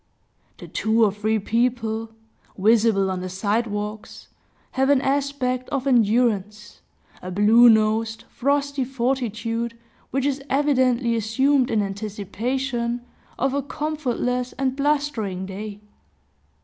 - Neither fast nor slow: No, slow, 115 wpm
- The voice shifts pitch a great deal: No, average, 3.8 semitones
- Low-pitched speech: No, high, 235 Hz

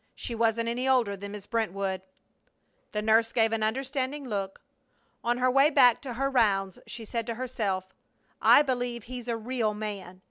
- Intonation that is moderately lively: Yes, average, 3.2 semitones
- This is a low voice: No, high, 230 Hz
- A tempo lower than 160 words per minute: No, average, 175 wpm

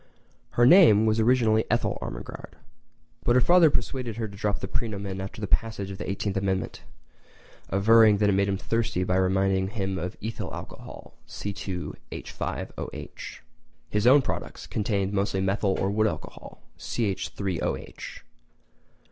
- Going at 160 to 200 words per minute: No, average, 140 wpm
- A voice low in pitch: Yes, low, 100 Hz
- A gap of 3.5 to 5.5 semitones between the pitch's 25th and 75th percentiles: No, average, 2.8 semitones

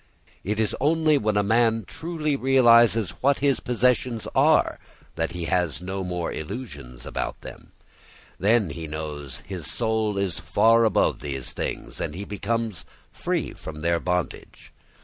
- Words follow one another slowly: No, average, 150 wpm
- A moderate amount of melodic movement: No, wide, 5.9 semitones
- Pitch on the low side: Yes, low, 105 Hz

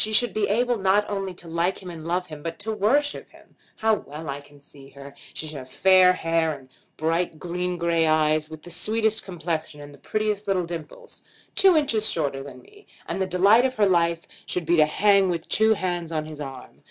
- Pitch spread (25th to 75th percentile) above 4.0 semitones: Yes, average, 4.7 semitones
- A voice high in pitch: No, medium, 175 Hz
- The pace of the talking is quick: Yes, fast, 220 wpm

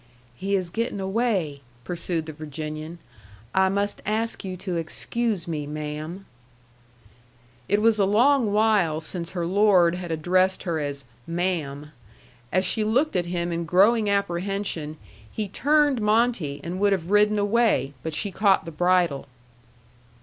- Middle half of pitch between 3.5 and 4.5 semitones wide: Yes, average, 4.1 semitones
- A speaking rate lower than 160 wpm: Yes, average, 145 wpm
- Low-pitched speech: No, medium, 185 Hz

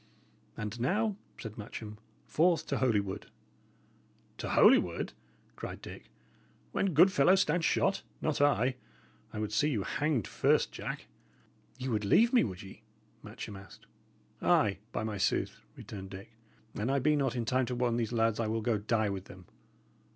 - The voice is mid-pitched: No, low, 115 Hz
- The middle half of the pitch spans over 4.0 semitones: Yes, wide, 5.5 semitones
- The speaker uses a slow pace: No, average, 165 wpm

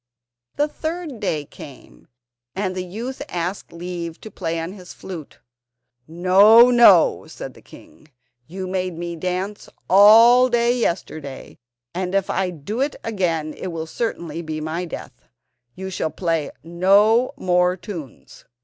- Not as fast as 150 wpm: Yes, average, 140 wpm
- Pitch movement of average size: Yes, average, 4.2 semitones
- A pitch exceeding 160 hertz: Yes, medium, 185 Hz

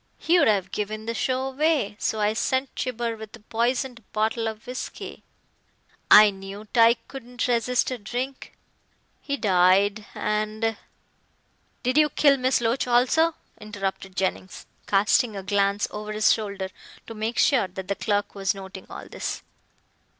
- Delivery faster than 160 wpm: No, average, 155 wpm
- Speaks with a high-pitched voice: Yes, high, 220 Hz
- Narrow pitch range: No, average, 3.5 semitones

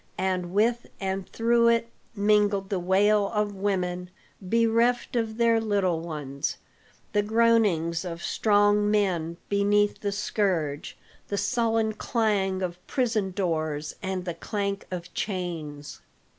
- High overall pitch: Yes, high, 200 Hz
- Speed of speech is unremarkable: No, slow, 125 wpm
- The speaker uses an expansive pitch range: No, average, 3.4 semitones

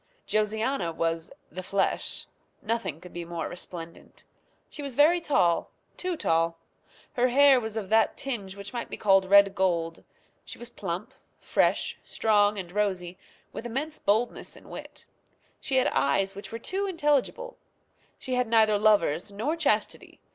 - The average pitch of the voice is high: Yes, high, 210 Hz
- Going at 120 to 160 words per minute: Yes, average, 155 wpm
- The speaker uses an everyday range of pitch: No, wide, 5.7 semitones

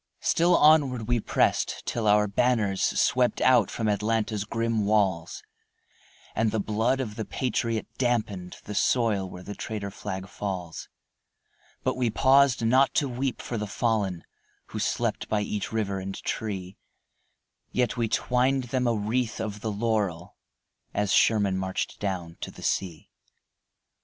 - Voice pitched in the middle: No, low, 110 Hz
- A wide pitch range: No, average, 3.5 semitones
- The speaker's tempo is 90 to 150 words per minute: Yes, average, 145 wpm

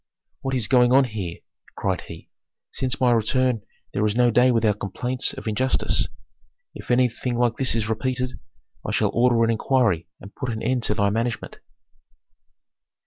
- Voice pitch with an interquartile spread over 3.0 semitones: No, narrow, 2.6 semitones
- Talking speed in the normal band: Yes, average, 165 wpm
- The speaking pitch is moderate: No, low, 120 Hz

